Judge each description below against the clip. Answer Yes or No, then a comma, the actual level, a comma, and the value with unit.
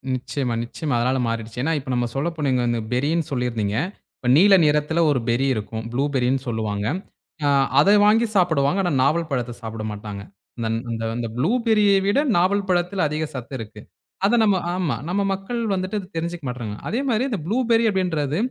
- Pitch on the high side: No, medium, 145 Hz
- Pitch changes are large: Yes, wide, 7.6 semitones